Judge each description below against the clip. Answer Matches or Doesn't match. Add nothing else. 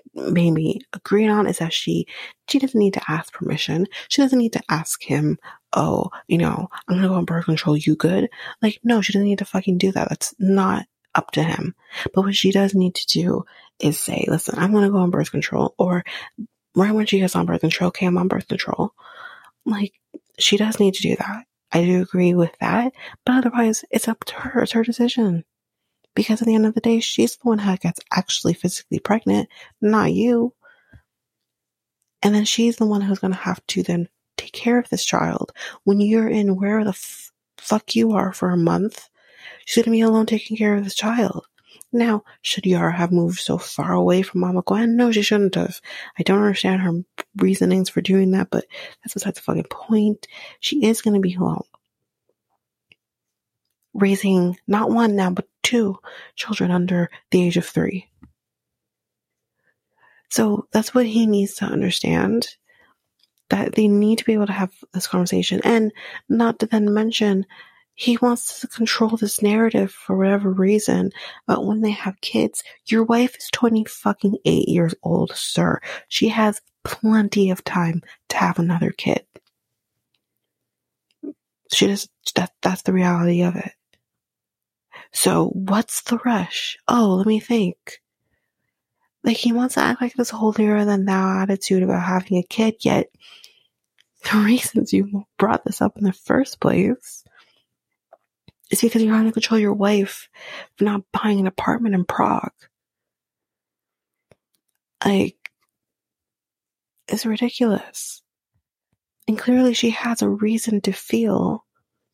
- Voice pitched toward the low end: Doesn't match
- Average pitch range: Matches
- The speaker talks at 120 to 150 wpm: Doesn't match